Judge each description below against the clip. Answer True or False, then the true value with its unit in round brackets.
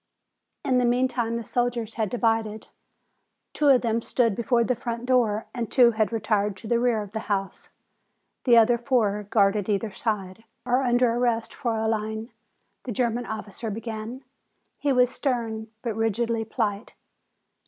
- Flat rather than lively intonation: True (2.0 semitones)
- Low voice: False (230 Hz)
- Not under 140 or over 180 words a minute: True (155 wpm)